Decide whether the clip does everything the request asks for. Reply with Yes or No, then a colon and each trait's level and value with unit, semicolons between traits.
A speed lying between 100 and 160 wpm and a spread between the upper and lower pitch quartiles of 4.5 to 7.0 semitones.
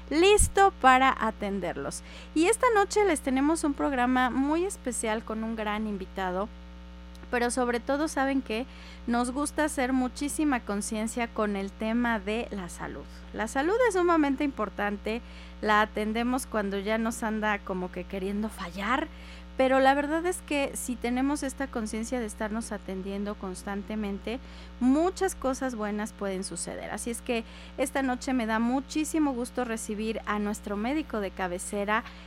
Yes: average, 150 wpm; average, 4.8 semitones